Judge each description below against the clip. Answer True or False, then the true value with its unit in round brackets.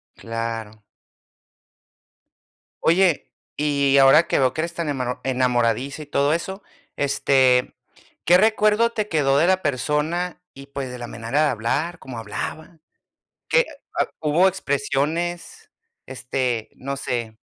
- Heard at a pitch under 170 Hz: True (140 Hz)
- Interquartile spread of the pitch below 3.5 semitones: False (5.1 semitones)